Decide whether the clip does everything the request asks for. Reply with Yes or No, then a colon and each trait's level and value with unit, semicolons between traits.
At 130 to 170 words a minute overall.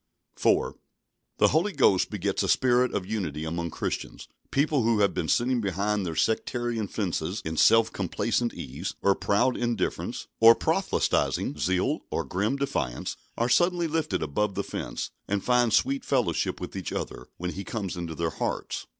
Yes: average, 165 wpm